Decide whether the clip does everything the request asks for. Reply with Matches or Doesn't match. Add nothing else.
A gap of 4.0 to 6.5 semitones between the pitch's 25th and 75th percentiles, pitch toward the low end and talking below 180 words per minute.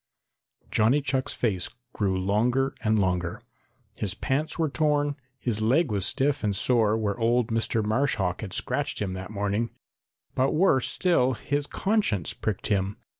Matches